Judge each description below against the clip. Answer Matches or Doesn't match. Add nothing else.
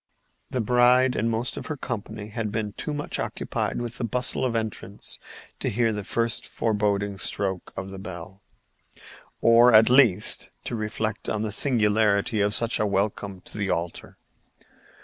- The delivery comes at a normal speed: Matches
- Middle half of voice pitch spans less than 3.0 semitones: Matches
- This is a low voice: Matches